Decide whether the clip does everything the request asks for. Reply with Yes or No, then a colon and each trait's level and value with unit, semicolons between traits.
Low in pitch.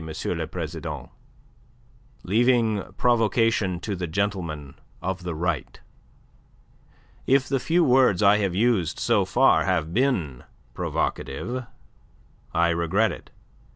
Yes: low, 100 Hz